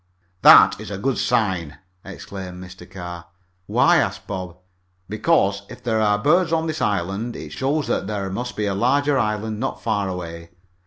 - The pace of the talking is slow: No, average, 170 wpm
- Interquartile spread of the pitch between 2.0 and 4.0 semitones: No, average, 5.0 semitones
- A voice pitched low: Yes, low, 105 Hz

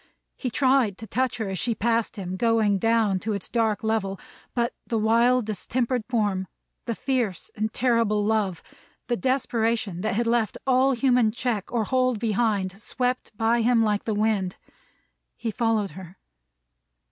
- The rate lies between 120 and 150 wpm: No, average, 160 wpm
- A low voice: No, high, 225 Hz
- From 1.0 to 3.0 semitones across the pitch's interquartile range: Yes, average, 2.7 semitones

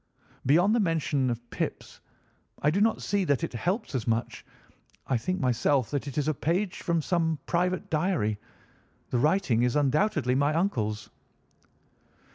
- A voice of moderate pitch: Yes, medium, 150 Hz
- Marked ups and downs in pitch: Yes, wide, 6.1 semitones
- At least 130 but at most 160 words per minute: Yes, average, 155 wpm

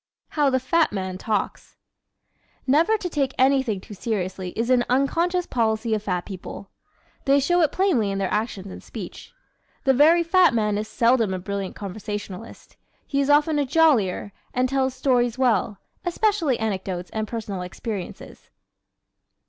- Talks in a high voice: Yes, high, 235 Hz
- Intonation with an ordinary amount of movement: No, wide, 5.7 semitones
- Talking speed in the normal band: Yes, average, 155 wpm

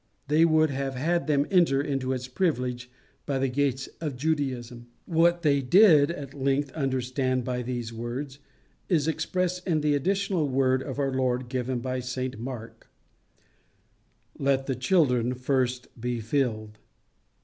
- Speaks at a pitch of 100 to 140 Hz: Yes, low, 135 Hz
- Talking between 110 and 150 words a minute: Yes, average, 145 wpm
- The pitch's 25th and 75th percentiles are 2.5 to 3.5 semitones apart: Yes, average, 3.0 semitones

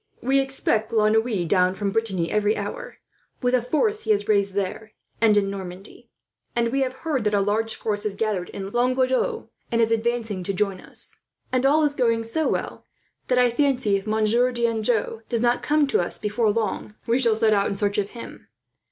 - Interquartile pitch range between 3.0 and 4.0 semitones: Yes, average, 3.3 semitones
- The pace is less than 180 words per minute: No, fast, 205 wpm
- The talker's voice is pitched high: Yes, high, 220 Hz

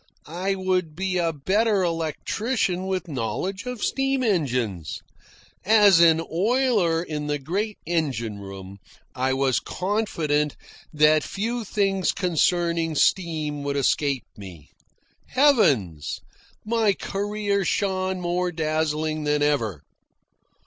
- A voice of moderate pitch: Yes, medium, 170 Hz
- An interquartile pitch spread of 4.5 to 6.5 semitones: Yes, average, 5.1 semitones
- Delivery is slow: Yes, slow, 110 wpm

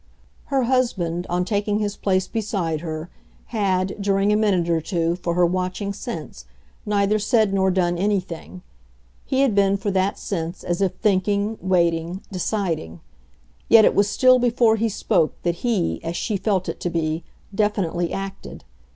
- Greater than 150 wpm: Yes, average, 160 wpm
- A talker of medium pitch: No, high, 195 Hz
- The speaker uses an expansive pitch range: No, average, 3.2 semitones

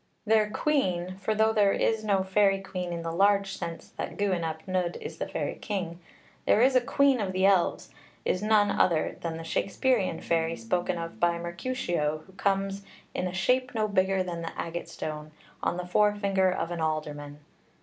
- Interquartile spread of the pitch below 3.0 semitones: No, average, 3.4 semitones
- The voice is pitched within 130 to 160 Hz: No, medium, 185 Hz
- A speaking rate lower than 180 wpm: No, average, 185 wpm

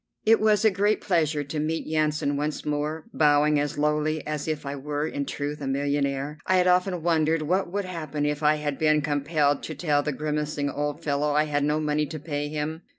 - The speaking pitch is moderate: Yes, medium, 150 Hz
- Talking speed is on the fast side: Yes, fast, 215 wpm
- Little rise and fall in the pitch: Yes, narrow, 1.4 semitones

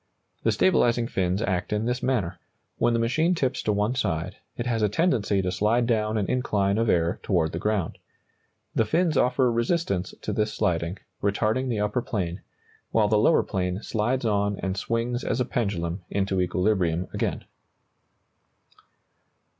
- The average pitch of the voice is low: Yes, low, 105 Hz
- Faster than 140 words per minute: Yes, average, 160 wpm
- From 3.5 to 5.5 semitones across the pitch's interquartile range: Yes, average, 4.1 semitones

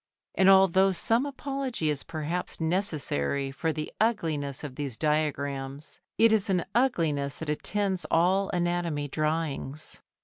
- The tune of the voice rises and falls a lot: No, average, 4.7 semitones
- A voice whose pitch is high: No, medium, 160 Hz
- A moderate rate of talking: No, slow, 130 wpm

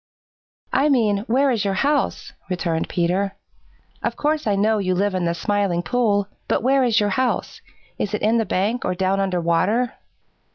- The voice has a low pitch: No, high, 205 Hz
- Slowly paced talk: No, average, 180 wpm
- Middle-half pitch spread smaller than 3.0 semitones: No, average, 4.2 semitones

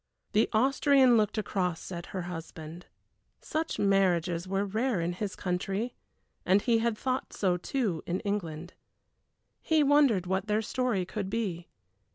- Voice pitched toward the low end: No, high, 195 Hz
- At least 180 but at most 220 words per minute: No, average, 145 wpm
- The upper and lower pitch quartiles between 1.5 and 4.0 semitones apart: No, average, 4.5 semitones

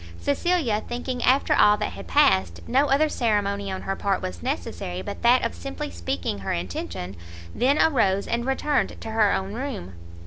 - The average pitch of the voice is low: No, high, 200 Hz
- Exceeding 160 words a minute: Yes, average, 175 wpm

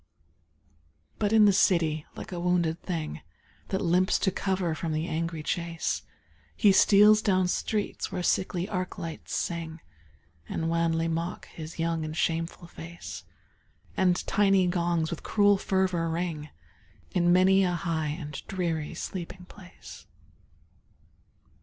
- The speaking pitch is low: No, medium, 175 Hz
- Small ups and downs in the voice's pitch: Yes, narrow, 2.3 semitones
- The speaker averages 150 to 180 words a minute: No, slow, 135 wpm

